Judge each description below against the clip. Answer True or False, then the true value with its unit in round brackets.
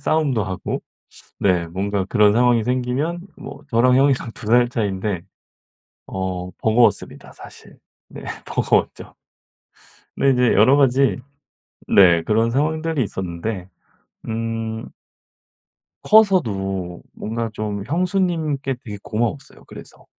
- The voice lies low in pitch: True (115 Hz)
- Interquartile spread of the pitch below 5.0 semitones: False (5.3 semitones)